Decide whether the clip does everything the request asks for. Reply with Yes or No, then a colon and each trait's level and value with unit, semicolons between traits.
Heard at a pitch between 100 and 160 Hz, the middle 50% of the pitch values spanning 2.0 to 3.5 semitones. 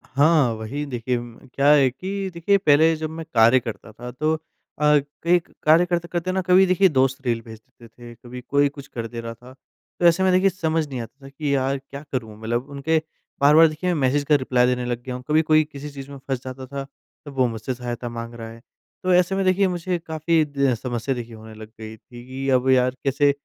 No: low, 135 Hz; average, 4.6 semitones